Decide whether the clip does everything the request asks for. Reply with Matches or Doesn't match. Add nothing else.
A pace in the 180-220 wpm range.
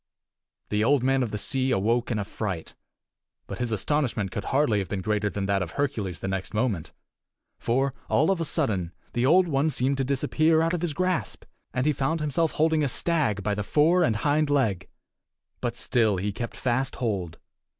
Matches